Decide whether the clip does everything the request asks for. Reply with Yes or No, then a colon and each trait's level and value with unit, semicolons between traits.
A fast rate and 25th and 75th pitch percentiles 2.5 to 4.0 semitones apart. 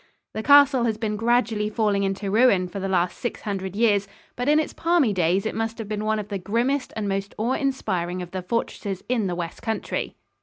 Yes: fast, 220 wpm; average, 3.4 semitones